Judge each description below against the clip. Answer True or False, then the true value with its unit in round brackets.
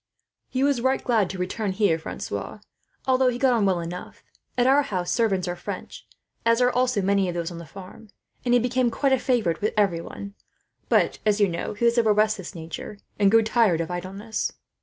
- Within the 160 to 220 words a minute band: True (200 wpm)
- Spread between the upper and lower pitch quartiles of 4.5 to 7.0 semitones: True (4.9 semitones)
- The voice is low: False (210 Hz)